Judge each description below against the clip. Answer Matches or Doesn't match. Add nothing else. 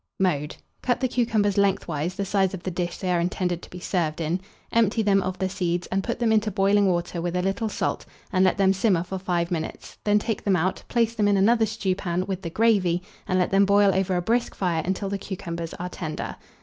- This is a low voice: Doesn't match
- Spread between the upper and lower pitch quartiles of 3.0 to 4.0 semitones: Doesn't match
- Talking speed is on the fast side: Matches